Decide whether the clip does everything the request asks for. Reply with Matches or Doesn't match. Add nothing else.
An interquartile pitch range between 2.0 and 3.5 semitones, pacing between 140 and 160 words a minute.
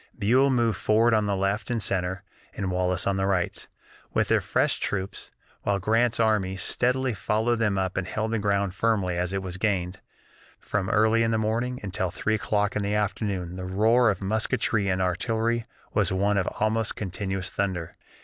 Doesn't match